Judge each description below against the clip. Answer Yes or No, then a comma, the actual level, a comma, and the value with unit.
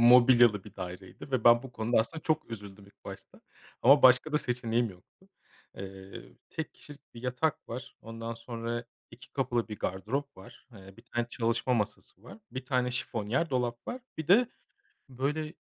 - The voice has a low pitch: Yes, low, 120 Hz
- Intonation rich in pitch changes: No, average, 2.8 semitones